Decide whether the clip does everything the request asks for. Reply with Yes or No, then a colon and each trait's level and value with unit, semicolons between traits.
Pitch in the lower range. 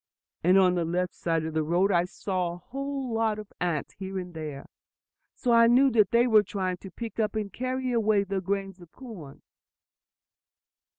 No: high, 195 Hz